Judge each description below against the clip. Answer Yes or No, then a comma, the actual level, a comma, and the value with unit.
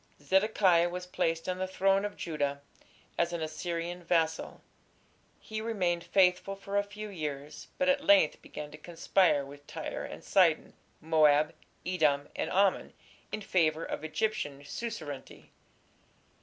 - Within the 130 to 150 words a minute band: Yes, average, 140 wpm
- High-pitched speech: No, medium, 175 Hz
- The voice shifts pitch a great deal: No, average, 4.2 semitones